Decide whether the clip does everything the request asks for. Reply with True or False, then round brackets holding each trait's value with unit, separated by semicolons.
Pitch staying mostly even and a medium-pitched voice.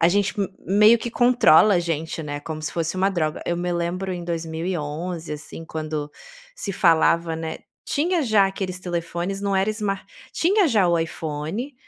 False (3.6 semitones; 175 Hz)